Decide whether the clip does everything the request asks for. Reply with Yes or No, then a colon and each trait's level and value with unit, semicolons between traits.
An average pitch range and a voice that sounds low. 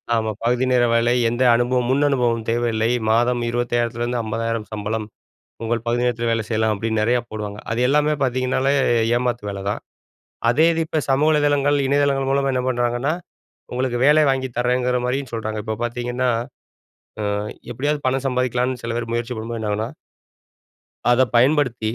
No: narrow, 2.2 semitones; low, 120 Hz